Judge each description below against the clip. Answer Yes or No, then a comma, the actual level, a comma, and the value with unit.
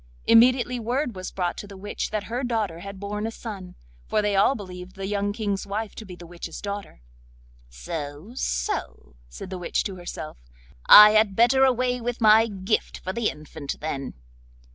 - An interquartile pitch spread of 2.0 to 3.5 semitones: No, average, 4.0 semitones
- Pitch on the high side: Yes, high, 200 Hz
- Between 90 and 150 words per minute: No, average, 180 wpm